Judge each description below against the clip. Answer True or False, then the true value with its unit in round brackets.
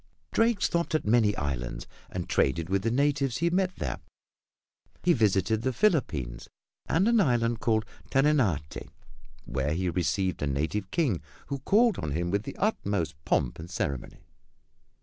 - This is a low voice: True (110 Hz)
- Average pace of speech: True (150 wpm)